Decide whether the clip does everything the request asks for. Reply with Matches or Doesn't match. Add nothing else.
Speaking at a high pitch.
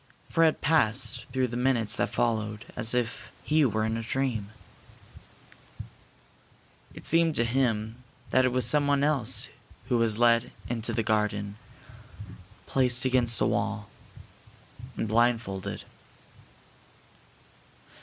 Doesn't match